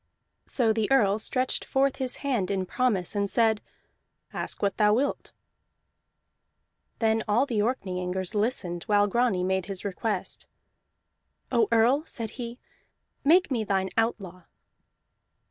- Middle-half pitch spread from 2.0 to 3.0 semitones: No, average, 4.0 semitones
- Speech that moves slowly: Yes, slow, 130 wpm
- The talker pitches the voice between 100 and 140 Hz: No, high, 220 Hz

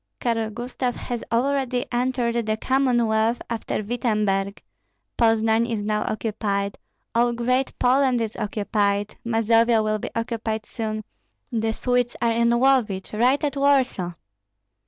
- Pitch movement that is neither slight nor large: No, narrow, 2.2 semitones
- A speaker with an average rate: No, slow, 125 wpm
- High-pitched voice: Yes, high, 230 Hz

